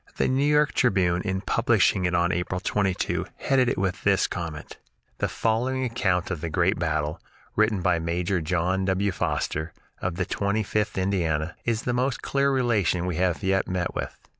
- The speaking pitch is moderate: No, very low, 95 Hz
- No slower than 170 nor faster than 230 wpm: Yes, average, 180 wpm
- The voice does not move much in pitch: No, average, 4.0 semitones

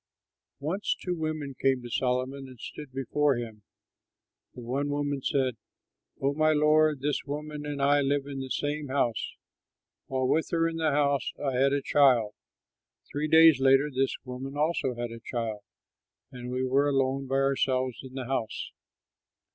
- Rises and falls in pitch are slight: Yes, narrow, 2.3 semitones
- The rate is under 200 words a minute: Yes, average, 165 wpm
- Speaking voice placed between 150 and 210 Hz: No, low, 135 Hz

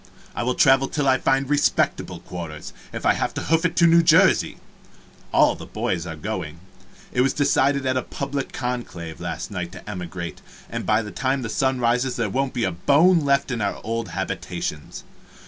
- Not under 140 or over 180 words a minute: No, average, 190 wpm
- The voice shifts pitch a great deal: Yes, wide, 5.7 semitones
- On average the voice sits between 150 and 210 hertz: No, low, 125 Hz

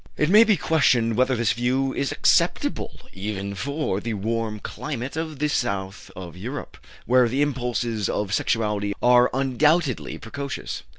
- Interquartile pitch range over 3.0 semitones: Yes, average, 4.7 semitones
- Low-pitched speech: Yes, low, 120 Hz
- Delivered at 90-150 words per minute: Yes, average, 145 wpm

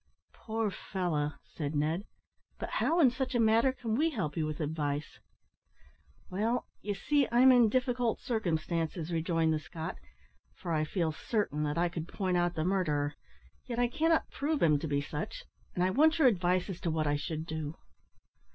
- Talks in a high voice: No, medium, 180 Hz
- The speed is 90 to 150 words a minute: No, average, 180 wpm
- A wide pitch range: Yes, wide, 7.1 semitones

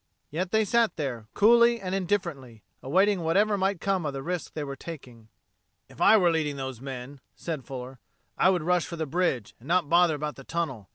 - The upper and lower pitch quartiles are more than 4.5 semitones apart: Yes, wide, 5.6 semitones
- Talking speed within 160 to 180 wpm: No, fast, 205 wpm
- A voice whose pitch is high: No, medium, 165 Hz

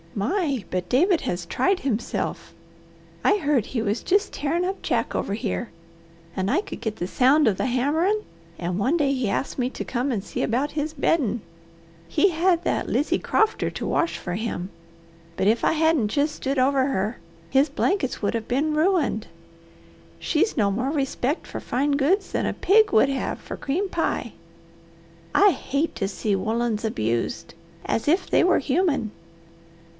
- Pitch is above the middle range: Yes, very high, 275 Hz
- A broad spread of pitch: Yes, wide, 6.7 semitones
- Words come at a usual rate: Yes, average, 175 wpm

